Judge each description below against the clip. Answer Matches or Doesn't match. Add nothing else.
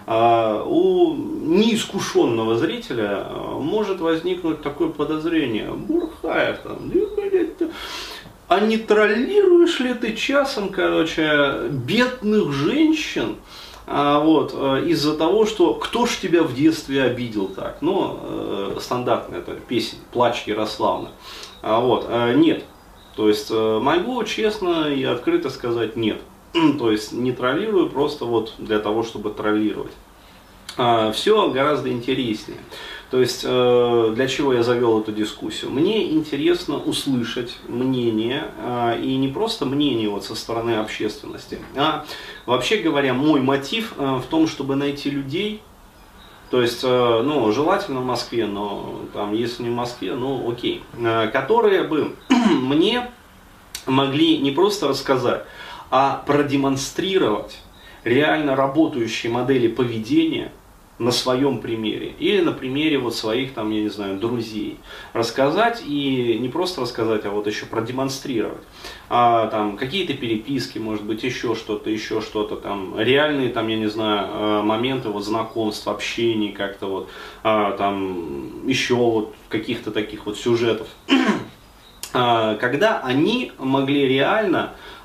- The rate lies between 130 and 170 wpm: Doesn't match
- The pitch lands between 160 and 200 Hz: Doesn't match